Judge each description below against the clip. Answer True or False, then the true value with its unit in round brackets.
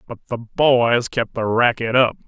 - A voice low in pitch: True (120 Hz)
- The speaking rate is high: False (185 wpm)